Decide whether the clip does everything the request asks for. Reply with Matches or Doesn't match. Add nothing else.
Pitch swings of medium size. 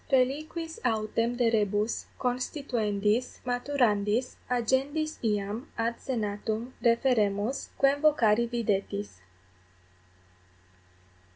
Matches